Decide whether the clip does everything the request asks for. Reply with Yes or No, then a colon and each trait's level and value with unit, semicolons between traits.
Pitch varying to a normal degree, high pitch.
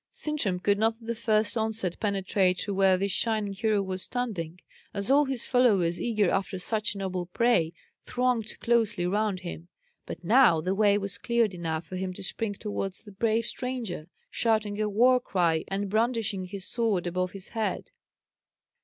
Yes: average, 3.5 semitones; high, 205 Hz